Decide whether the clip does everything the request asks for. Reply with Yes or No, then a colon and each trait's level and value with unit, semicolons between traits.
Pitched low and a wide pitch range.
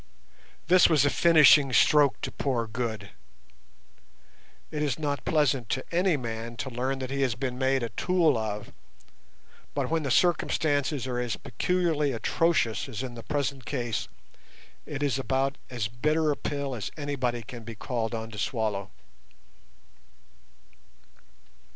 No: low, 130 Hz; average, 3.9 semitones